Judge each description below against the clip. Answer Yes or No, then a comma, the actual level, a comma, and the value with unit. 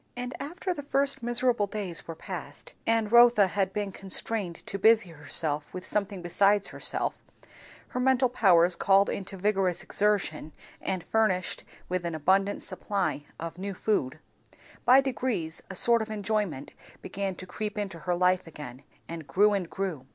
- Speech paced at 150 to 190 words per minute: Yes, average, 160 wpm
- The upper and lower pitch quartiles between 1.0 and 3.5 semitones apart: No, average, 3.9 semitones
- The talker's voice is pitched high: Yes, high, 195 Hz